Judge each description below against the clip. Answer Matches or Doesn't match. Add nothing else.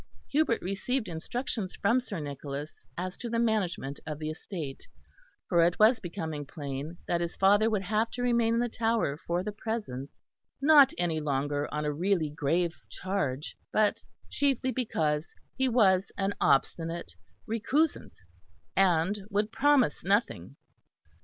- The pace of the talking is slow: Doesn't match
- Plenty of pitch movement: Matches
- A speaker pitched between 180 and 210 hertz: Matches